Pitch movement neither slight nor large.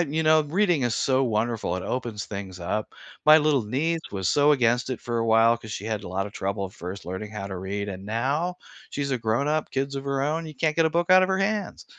No: wide, 6.6 semitones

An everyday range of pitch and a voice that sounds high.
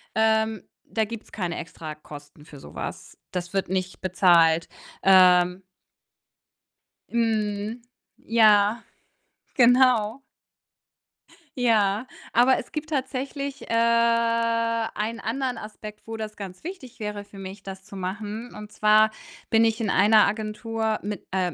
Yes: average, 3.1 semitones; high, 215 Hz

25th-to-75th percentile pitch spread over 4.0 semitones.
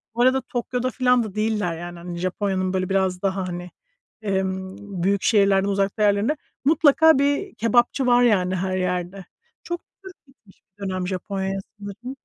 Yes: average, 4.5 semitones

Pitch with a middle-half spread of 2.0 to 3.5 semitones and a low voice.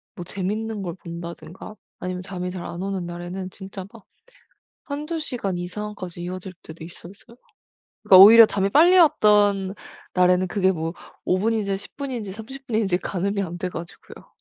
No: average, 3.1 semitones; high, 195 Hz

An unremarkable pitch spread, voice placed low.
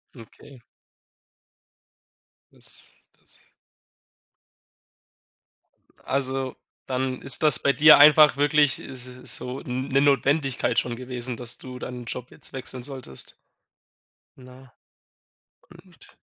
No: narrow, 2.1 semitones; low, 130 Hz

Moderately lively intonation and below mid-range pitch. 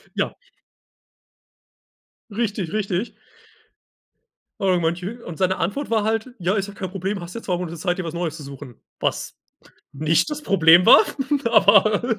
No: average, 3.9 semitones; high, 190 Hz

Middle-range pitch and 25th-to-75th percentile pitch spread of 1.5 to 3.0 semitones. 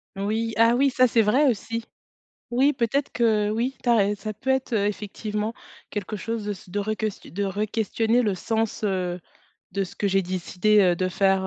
No: high, 215 Hz; narrow, 2.6 semitones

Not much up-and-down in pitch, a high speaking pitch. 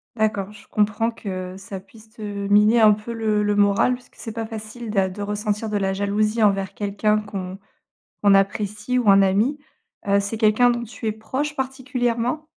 Yes: narrow, 2.2 semitones; high, 210 Hz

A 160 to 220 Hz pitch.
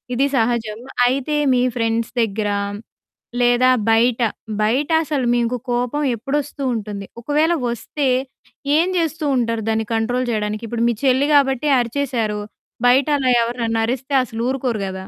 No: high, 245 Hz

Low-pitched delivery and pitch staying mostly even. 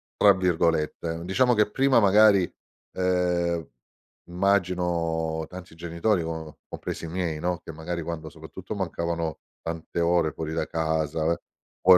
Yes: very low, 85 Hz; narrow, 2.2 semitones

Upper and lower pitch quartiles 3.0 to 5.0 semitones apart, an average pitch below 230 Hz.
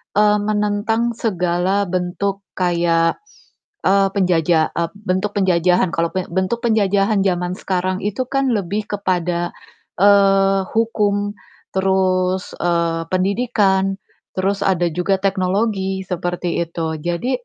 No: narrow, 2.4 semitones; high, 190 Hz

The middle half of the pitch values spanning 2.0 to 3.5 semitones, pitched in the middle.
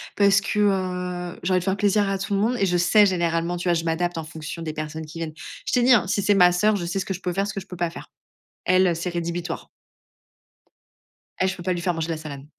Yes: average, 2.7 semitones; medium, 180 Hz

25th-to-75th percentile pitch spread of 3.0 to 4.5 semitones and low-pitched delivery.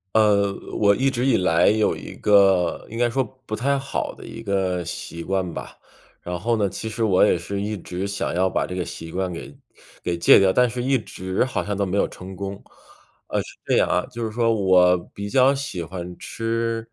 Yes: average, 3.9 semitones; low, 100 Hz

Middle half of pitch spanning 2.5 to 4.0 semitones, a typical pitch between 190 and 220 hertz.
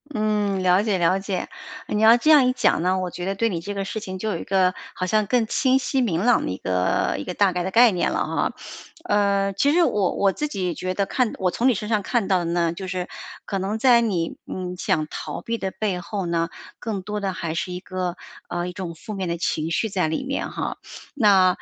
Yes: average, 3.1 semitones; high, 195 Hz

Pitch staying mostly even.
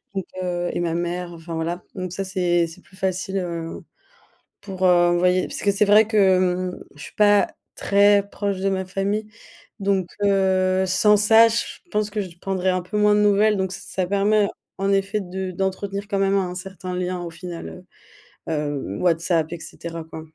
Yes: narrow, 2.2 semitones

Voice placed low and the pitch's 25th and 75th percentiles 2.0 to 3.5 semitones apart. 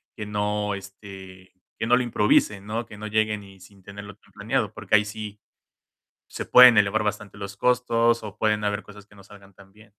No: low, 105 Hz; narrow, 1.4 semitones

